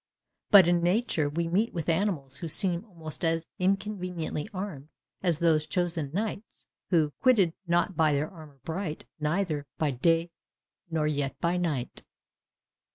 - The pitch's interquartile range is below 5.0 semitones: Yes, average, 3.2 semitones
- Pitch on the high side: No, medium, 170 Hz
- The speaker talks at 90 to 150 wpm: Yes, average, 140 wpm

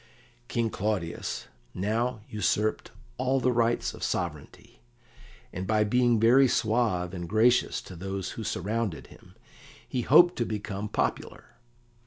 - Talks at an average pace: No, slow, 130 wpm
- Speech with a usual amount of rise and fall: Yes, average, 3.9 semitones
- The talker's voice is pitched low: Yes, low, 110 Hz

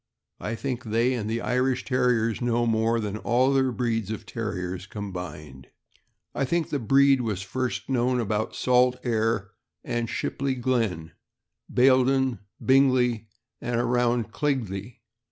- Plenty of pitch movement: No, average, 2.8 semitones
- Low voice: Yes, low, 120 Hz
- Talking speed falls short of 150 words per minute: Yes, average, 140 wpm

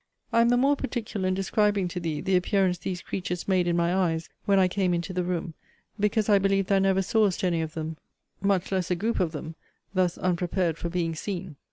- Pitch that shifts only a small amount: Yes, narrow, 2.3 semitones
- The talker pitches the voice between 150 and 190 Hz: Yes, medium, 185 Hz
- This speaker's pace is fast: Yes, fast, 220 wpm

